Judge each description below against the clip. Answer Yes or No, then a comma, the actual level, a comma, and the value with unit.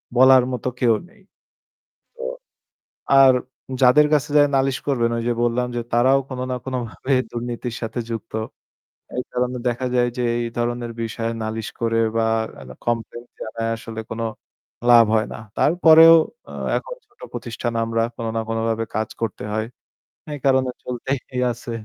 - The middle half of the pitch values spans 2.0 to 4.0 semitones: Yes, narrow, 2.4 semitones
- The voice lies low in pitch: Yes, low, 120 Hz